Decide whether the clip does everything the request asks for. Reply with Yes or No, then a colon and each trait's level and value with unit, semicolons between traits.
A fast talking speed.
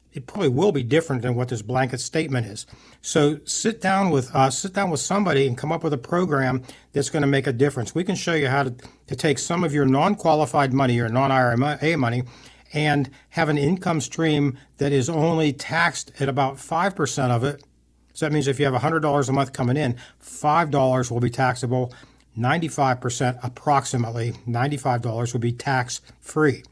No: average, 190 wpm